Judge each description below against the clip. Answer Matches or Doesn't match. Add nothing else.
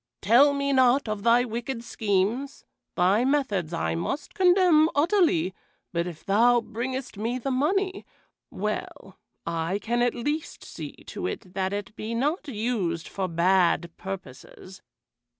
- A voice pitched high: Matches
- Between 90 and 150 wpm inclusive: Matches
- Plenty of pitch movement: Matches